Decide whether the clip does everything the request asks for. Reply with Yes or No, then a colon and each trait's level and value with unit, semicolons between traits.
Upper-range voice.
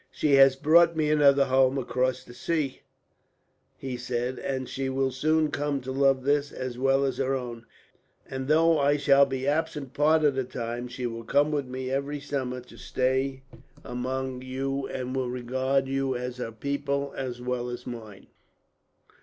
No: low, 135 Hz